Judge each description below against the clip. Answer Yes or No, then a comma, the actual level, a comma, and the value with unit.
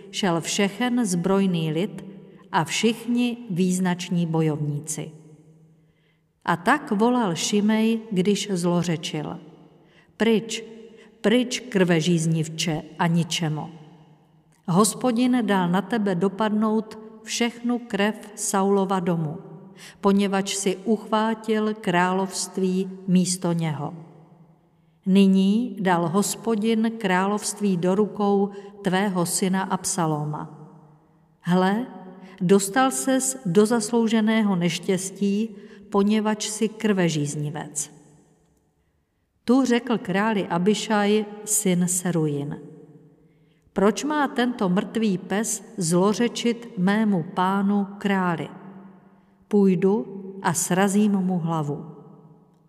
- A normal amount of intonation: Yes, average, 4.1 semitones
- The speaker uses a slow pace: Yes, slow, 85 wpm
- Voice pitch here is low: No, high, 190 Hz